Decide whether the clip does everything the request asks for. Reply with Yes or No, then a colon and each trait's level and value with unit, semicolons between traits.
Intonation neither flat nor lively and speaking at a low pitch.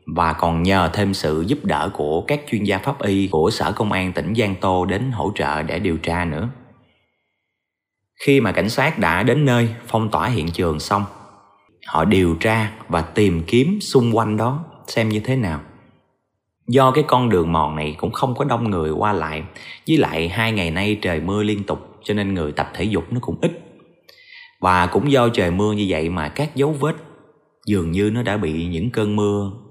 No: wide, 5.9 semitones; low, 105 Hz